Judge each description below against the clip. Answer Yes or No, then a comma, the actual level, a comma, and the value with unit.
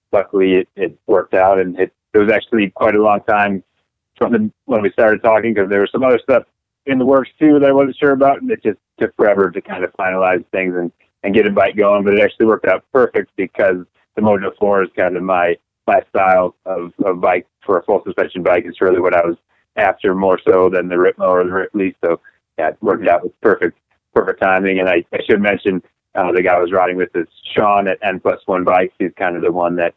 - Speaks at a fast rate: Yes, fast, 245 wpm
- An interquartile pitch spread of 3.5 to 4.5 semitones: No, average, 2.8 semitones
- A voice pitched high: No, very low, 95 Hz